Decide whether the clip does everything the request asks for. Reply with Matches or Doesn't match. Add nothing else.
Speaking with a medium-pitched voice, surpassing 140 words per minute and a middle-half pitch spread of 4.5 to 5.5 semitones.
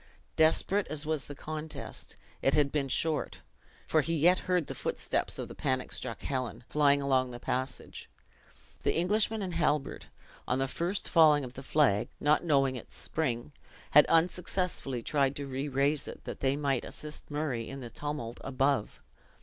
Doesn't match